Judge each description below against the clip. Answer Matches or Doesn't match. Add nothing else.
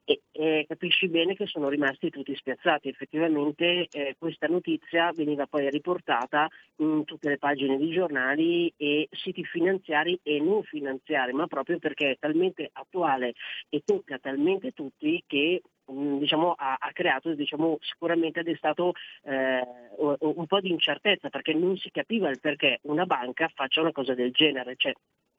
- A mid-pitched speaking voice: Matches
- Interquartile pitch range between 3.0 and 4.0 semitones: Matches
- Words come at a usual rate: Matches